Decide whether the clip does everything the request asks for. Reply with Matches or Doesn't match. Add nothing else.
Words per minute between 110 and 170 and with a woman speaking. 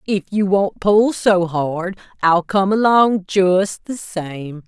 Matches